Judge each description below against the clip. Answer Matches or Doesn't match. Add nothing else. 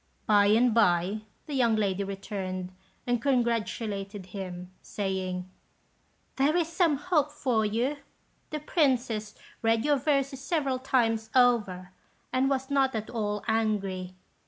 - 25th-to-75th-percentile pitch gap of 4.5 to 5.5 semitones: Matches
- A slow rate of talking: Matches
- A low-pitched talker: Doesn't match